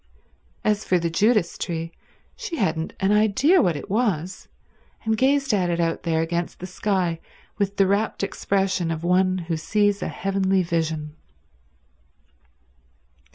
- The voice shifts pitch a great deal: No, average, 3.6 semitones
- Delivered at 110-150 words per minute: Yes, average, 145 wpm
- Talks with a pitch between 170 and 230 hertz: Yes, high, 190 Hz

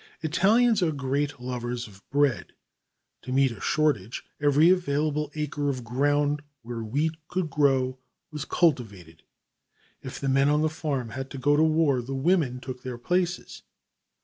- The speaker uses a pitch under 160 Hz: Yes, medium, 140 Hz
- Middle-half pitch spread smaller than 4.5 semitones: Yes, average, 3.4 semitones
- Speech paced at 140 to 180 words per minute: Yes, average, 150 wpm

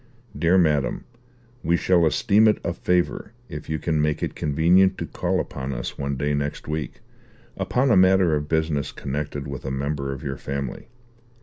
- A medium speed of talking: Yes, average, 180 wpm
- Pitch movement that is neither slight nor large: Yes, average, 3.9 semitones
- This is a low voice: Yes, very low, 75 Hz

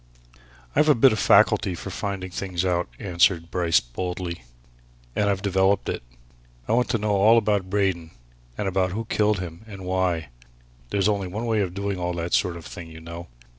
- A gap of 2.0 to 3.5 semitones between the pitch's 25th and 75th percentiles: Yes, average, 2.8 semitones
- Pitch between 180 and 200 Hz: No, very low, 95 Hz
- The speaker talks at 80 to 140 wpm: No, average, 195 wpm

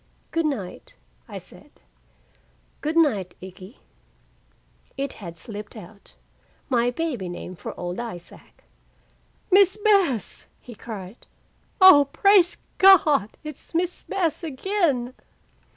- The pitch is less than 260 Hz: No, very high, 265 Hz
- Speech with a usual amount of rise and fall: No, wide, 8.9 semitones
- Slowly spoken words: Yes, slow, 105 wpm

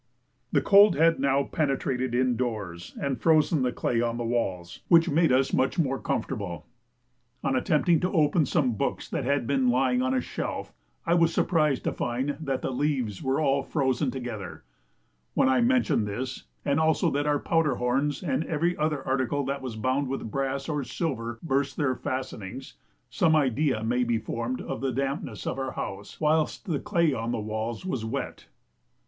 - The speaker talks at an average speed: Yes, average, 180 wpm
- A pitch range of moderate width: Yes, average, 3.6 semitones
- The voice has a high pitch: No, low, 135 Hz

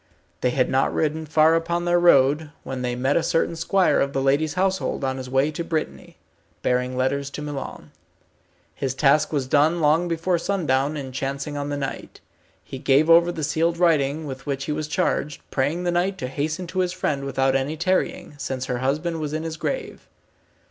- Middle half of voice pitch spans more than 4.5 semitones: No, average, 3.6 semitones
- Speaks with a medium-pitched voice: Yes, medium, 150 Hz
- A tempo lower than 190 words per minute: No, average, 195 wpm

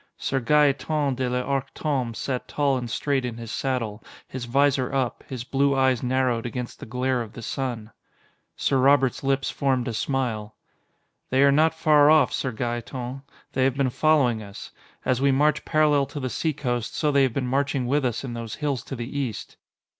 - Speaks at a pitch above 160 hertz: No, low, 130 Hz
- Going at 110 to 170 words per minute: No, average, 190 wpm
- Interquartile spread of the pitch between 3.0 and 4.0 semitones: No, narrow, 2.4 semitones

